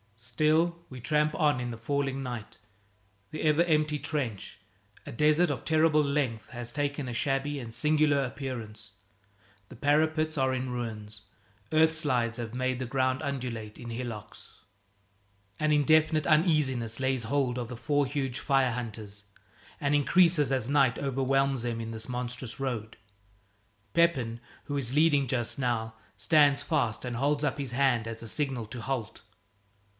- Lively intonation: No, average, 3.8 semitones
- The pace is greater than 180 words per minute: No, average, 150 wpm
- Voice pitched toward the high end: No, low, 130 Hz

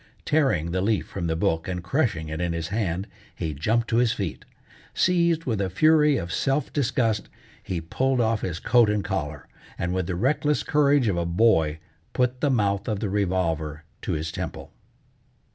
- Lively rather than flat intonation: Yes, wide, 6.7 semitones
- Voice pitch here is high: No, low, 100 Hz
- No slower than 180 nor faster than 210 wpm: Yes, average, 185 wpm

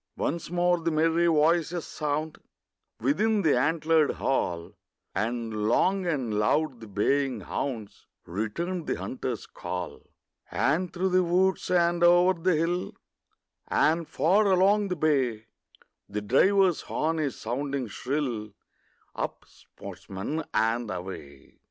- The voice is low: No, medium, 155 Hz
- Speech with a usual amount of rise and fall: No, wide, 6.9 semitones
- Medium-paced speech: No, slow, 120 wpm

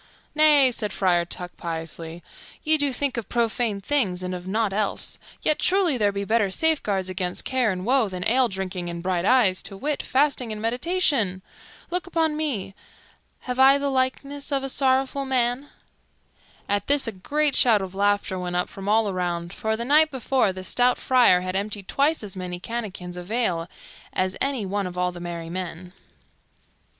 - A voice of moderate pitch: No, high, 215 Hz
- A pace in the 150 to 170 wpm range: No, average, 180 wpm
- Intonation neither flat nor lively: No, wide, 6.3 semitones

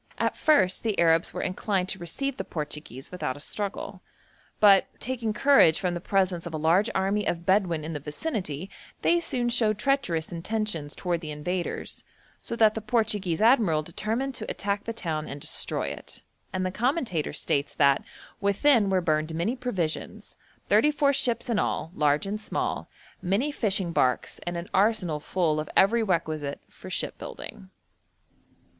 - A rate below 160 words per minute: No, average, 165 wpm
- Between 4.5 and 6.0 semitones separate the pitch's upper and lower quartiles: Yes, wide, 5.5 semitones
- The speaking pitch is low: No, medium, 185 Hz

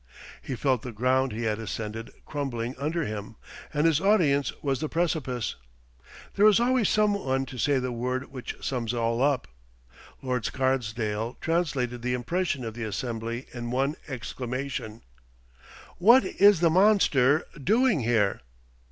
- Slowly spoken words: No, average, 145 wpm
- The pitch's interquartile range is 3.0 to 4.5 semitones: No, average, 4.9 semitones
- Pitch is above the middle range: No, low, 130 Hz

